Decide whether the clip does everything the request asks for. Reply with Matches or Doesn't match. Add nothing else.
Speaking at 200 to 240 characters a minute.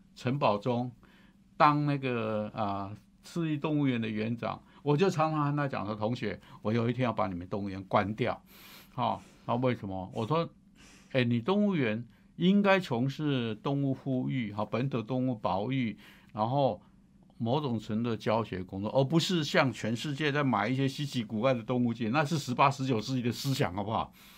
Doesn't match